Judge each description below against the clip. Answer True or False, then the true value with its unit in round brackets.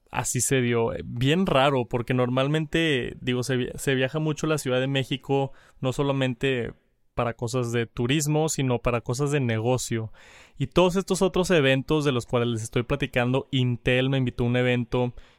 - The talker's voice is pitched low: True (130 Hz)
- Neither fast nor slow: True (170 wpm)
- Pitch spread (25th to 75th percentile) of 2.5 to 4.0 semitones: True (2.9 semitones)